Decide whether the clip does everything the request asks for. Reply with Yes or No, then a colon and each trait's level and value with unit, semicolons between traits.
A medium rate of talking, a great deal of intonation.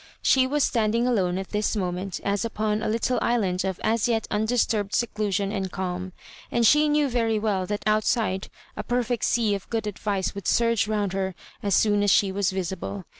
No: average, 190 wpm; average, 3.1 semitones